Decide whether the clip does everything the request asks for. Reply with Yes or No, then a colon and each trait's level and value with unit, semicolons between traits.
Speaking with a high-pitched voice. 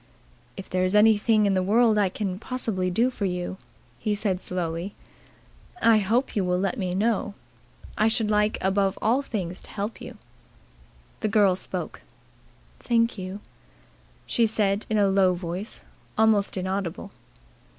Yes: high, 200 Hz